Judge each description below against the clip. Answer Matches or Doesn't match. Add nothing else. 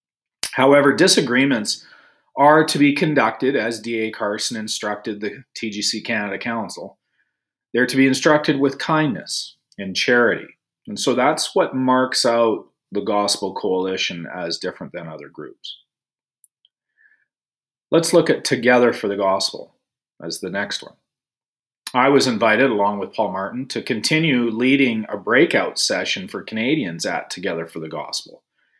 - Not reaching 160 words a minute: Matches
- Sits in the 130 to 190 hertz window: Doesn't match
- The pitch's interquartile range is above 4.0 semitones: Matches